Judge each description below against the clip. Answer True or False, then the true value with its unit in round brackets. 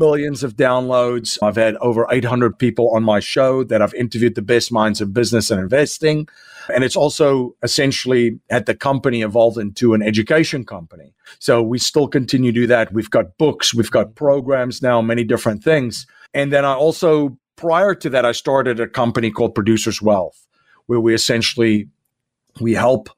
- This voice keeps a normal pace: True (180 wpm)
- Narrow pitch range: False (3.2 semitones)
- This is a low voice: True (120 Hz)